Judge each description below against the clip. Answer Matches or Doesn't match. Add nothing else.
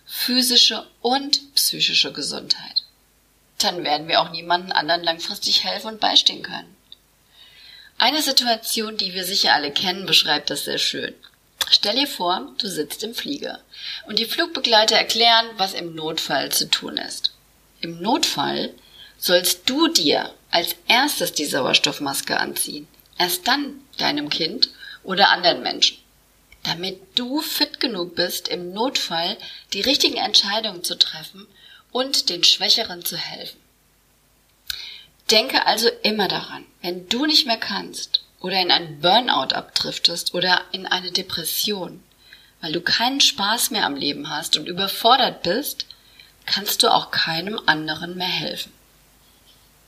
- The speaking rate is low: Doesn't match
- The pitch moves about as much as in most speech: Doesn't match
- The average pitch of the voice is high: Matches